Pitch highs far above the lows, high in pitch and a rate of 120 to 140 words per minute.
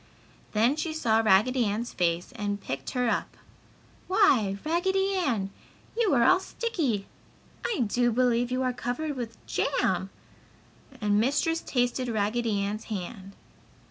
Yes: wide, 5.7 semitones; high, 240 Hz; slow, 135 wpm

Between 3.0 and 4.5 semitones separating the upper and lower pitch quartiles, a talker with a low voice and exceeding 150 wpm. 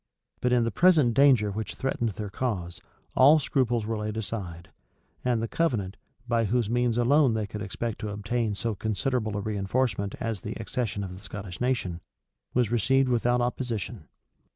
Yes: average, 3.3 semitones; low, 115 Hz; average, 170 wpm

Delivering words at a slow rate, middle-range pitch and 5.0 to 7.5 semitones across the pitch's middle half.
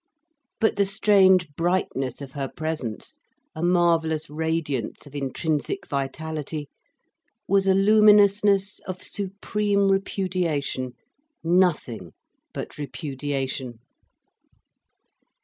Yes: slow, 85 wpm; medium, 165 Hz; wide, 5.4 semitones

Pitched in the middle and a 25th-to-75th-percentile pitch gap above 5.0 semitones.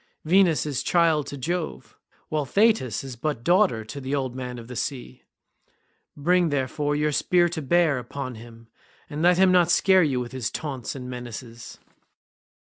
Yes: medium, 145 Hz; wide, 5.5 semitones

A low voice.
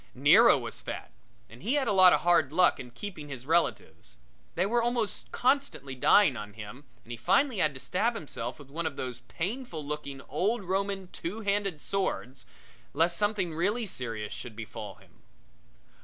No: medium, 170 Hz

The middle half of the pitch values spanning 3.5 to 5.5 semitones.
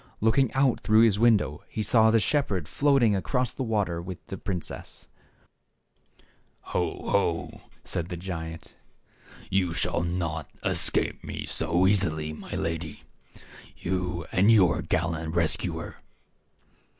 Yes: average, 4.9 semitones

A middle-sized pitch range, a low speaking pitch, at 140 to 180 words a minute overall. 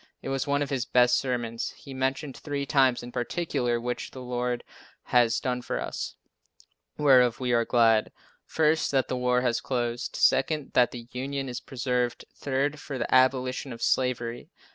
No: narrow, 1.9 semitones; low, 125 Hz; average, 170 wpm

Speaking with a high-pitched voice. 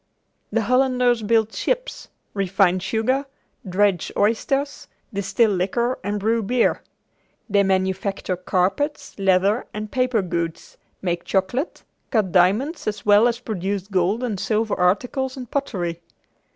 Yes: high, 210 Hz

